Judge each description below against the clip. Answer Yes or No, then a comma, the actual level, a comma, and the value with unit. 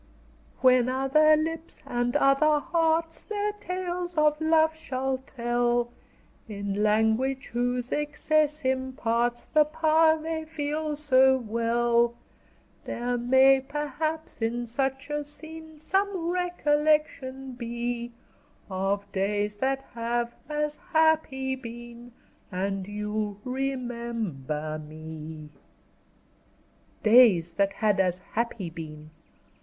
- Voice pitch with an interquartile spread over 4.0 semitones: Yes, average, 4.9 semitones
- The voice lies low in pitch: No, very high, 260 Hz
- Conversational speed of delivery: No, slow, 100 wpm